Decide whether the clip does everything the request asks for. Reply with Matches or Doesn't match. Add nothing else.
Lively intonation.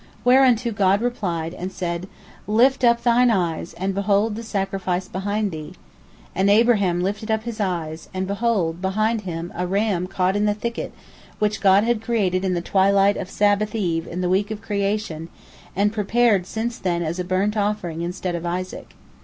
Doesn't match